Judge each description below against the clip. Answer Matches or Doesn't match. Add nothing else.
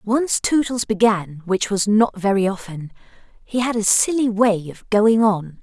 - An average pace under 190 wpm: Matches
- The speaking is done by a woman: Matches